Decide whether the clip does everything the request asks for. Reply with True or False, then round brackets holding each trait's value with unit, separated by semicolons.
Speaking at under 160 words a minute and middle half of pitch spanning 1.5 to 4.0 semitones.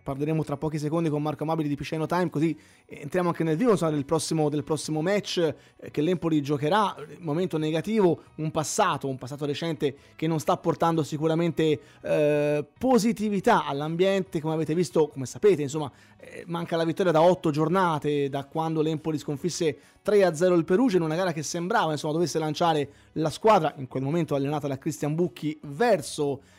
False (165 wpm; 2.7 semitones)